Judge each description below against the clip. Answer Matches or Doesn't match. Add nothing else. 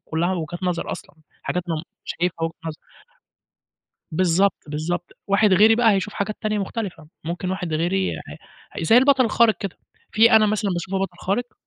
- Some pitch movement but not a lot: Matches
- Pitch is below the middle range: Doesn't match